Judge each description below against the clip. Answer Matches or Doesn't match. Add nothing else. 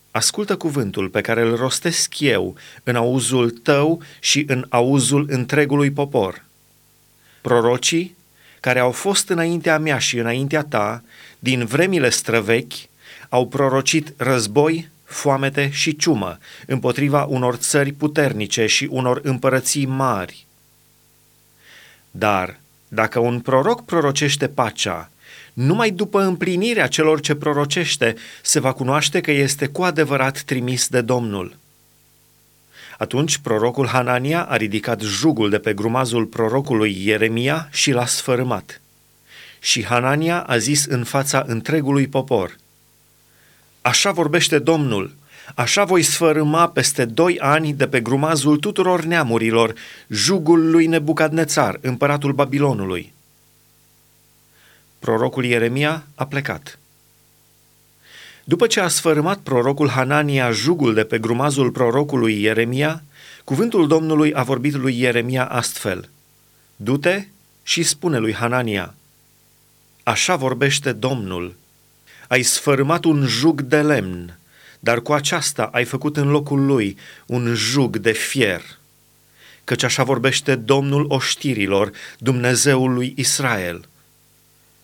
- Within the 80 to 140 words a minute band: Matches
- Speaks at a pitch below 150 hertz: Matches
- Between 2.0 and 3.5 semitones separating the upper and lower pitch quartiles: Doesn't match